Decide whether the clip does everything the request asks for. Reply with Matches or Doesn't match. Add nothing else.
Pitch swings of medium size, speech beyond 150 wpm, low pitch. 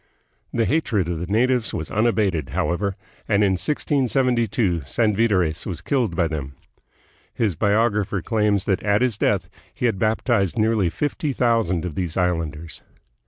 Doesn't match